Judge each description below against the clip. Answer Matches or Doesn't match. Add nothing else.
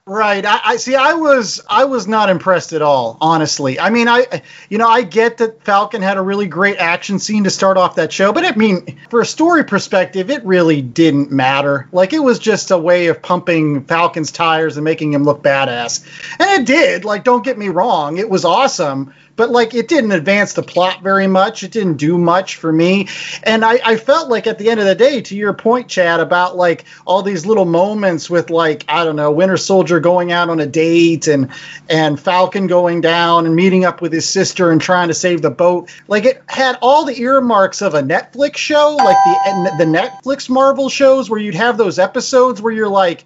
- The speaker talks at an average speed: Doesn't match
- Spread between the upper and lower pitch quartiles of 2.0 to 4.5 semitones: Doesn't match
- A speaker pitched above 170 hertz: Matches